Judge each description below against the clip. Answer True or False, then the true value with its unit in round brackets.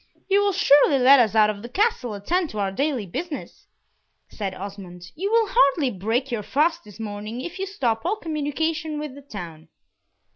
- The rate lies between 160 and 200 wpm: True (180 wpm)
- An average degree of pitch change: False (7.7 semitones)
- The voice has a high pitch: True (270 Hz)